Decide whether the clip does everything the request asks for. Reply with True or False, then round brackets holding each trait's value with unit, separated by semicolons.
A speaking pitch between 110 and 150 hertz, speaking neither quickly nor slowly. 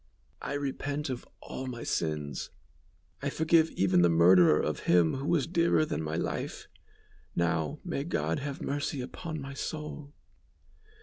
True (135 Hz; 145 wpm)